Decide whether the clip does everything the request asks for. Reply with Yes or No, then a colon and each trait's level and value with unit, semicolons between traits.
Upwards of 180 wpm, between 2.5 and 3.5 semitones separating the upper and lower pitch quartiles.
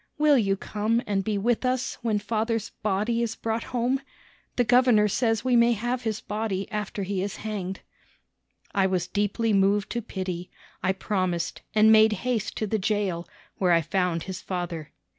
No: average, 175 wpm; average, 3.1 semitones